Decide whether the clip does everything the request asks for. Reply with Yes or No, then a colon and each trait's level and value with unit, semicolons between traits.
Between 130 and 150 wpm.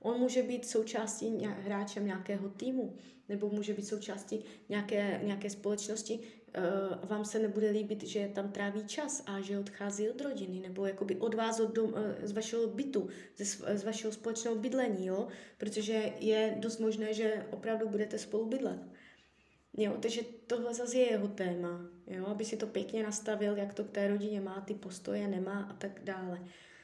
No: fast, 170 wpm